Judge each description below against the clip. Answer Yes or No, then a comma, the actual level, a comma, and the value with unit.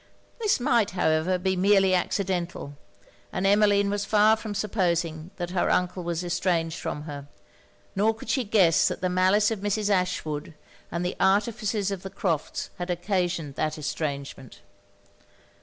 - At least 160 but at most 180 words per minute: No, average, 150 wpm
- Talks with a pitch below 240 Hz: Yes, medium, 185 Hz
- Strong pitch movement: No, average, 3.2 semitones